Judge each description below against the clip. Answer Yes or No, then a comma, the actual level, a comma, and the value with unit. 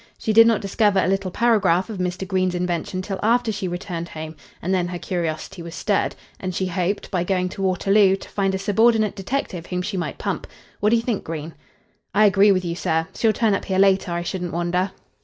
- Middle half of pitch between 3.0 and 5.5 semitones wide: No, narrow, 2.5 semitones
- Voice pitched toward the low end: No, high, 190 Hz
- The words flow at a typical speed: No, fast, 220 wpm